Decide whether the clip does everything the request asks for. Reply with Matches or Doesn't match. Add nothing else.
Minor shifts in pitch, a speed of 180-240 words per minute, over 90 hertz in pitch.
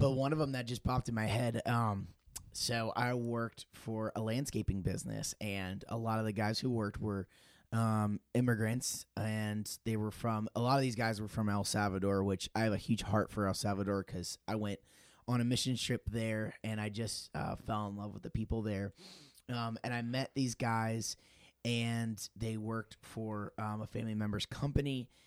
Matches